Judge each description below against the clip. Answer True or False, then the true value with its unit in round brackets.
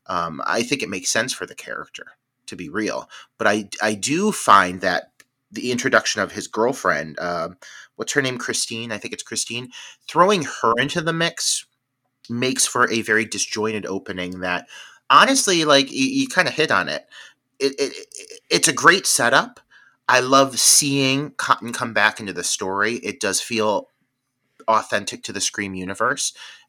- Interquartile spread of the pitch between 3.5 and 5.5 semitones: True (5.0 semitones)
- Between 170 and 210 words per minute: True (175 wpm)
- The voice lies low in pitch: True (125 Hz)